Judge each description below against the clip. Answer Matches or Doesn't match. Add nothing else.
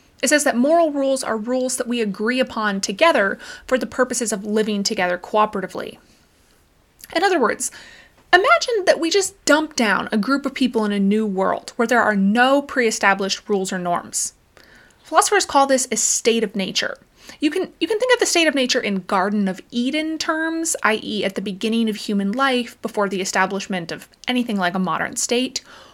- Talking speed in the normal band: Matches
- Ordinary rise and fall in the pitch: Doesn't match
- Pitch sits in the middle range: Doesn't match